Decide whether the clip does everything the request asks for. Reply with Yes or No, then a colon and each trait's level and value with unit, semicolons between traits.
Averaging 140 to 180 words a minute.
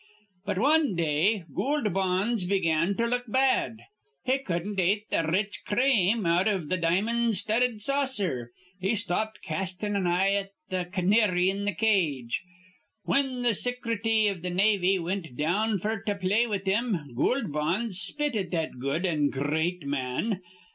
Yes: average, 160 wpm